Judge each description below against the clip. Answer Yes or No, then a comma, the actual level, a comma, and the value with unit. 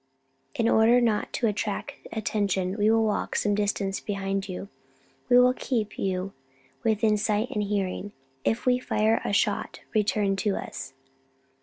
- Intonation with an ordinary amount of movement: No, narrow, 2.1 semitones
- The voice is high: Yes, high, 210 Hz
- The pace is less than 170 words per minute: Yes, average, 150 wpm